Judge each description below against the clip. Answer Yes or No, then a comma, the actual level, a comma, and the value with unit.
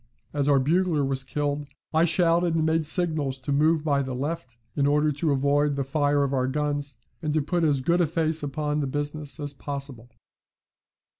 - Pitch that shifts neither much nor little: No, narrow, 2.2 semitones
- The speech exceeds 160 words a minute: Yes, average, 195 wpm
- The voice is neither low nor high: Yes, medium, 145 Hz